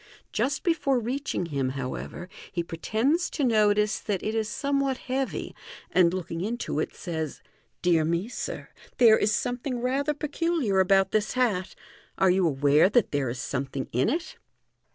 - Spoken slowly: No, average, 165 wpm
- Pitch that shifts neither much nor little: No, wide, 7.3 semitones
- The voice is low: No, high, 210 Hz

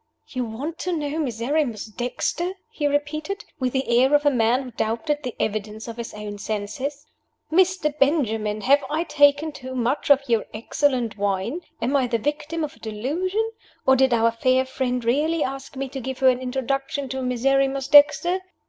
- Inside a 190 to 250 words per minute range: No, average, 180 wpm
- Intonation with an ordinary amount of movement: Yes, average, 3.9 semitones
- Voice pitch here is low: No, very high, 265 Hz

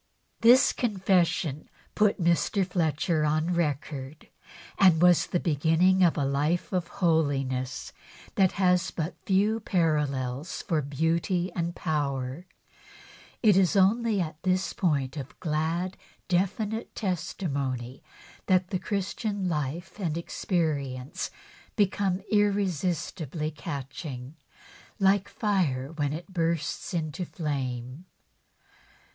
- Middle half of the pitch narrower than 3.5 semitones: No, average, 4.4 semitones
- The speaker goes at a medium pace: No, slow, 105 wpm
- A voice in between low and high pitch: Yes, medium, 170 Hz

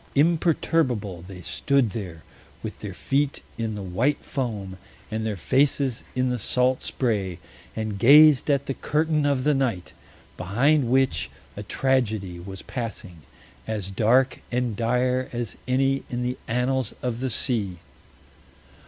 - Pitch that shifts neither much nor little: Yes, average, 4.5 semitones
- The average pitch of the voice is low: Yes, low, 125 Hz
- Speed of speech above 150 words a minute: No, average, 140 wpm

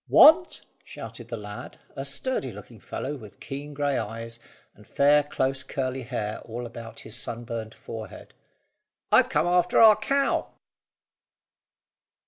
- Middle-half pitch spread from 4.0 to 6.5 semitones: Yes, average, 4.3 semitones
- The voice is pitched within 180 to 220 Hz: No, low, 130 Hz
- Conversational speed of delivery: No, slow, 130 wpm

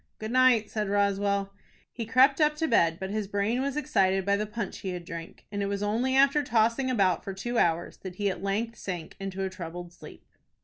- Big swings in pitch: No, average, 3.7 semitones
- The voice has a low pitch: No, high, 205 Hz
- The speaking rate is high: Yes, fast, 220 wpm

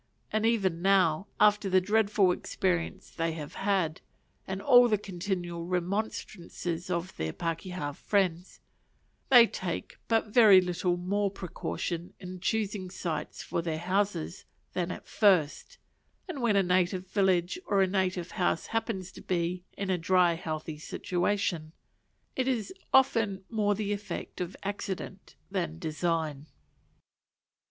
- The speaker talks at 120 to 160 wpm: Yes, slow, 135 wpm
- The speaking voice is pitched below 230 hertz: Yes, medium, 185 Hz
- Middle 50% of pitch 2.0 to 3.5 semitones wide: Yes, average, 2.9 semitones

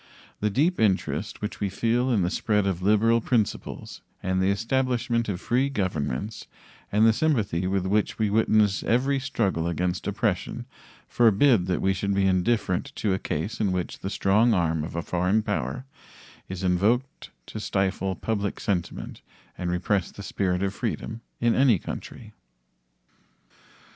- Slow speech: No, average, 155 wpm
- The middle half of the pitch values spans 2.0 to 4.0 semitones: Yes, average, 3.6 semitones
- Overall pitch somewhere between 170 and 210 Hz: No, low, 100 Hz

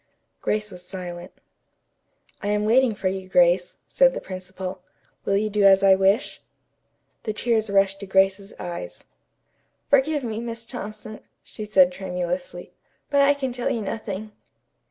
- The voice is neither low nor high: No, high, 200 Hz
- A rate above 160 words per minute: No, average, 150 wpm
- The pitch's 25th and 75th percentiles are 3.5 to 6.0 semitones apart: No, average, 3.1 semitones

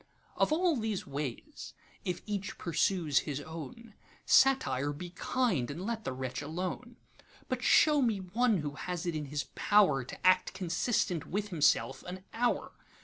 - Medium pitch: Yes, medium, 180 Hz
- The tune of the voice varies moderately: No, wide, 6.8 semitones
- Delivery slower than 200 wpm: Yes, average, 145 wpm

